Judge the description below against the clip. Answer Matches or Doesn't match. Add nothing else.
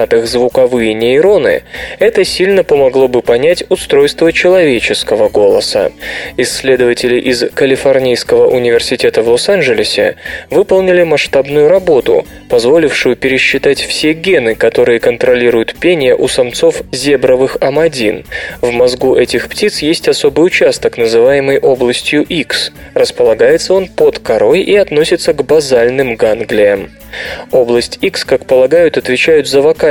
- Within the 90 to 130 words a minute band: Matches